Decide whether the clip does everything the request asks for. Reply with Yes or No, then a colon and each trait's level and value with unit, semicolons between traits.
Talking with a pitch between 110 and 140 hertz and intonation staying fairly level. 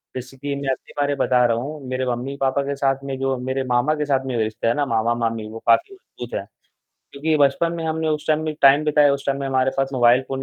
Yes: low, 135 Hz; narrow, 2.1 semitones